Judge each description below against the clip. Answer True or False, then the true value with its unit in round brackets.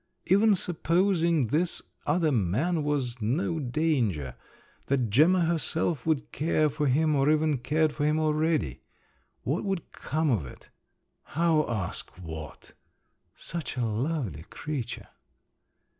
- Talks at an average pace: False (125 wpm)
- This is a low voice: False (150 Hz)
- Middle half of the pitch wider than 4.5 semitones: True (5.1 semitones)